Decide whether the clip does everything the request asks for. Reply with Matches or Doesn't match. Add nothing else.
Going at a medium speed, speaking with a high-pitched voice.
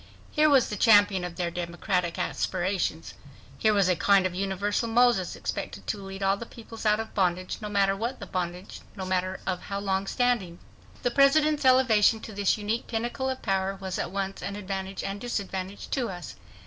Matches